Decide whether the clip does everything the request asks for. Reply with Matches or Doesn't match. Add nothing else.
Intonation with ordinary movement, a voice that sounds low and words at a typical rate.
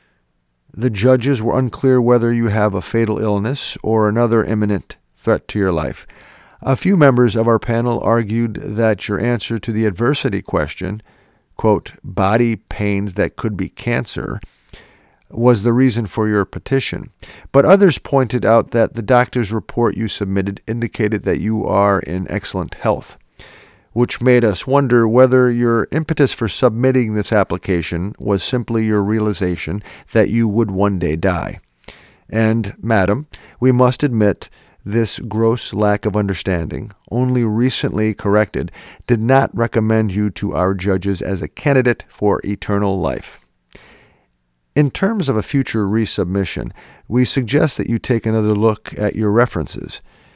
Matches